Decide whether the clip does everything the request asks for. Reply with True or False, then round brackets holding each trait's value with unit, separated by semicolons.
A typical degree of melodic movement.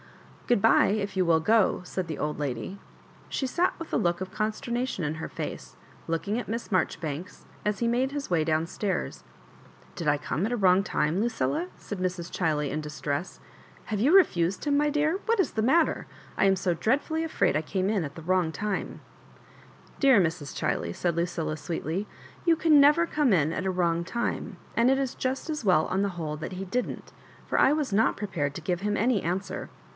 False (6.5 semitones)